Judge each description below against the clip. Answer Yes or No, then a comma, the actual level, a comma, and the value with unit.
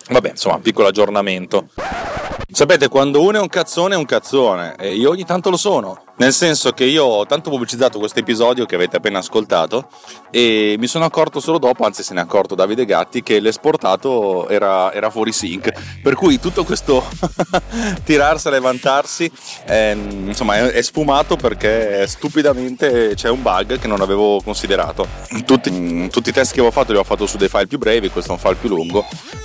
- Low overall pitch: Yes, low, 125 Hz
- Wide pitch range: Yes, wide, 6.1 semitones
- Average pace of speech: No, fast, 190 wpm